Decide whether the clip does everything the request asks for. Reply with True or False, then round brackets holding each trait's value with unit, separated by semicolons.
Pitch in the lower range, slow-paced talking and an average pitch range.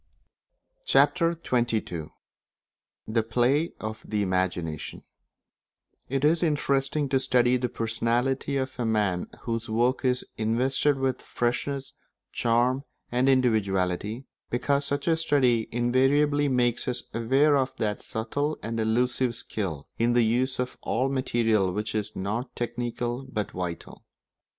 True (120 Hz; 125 wpm; 3.2 semitones)